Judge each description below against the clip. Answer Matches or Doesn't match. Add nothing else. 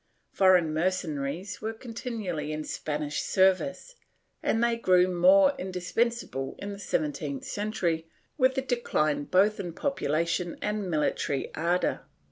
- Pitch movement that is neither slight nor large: Doesn't match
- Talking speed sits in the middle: Doesn't match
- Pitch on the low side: Doesn't match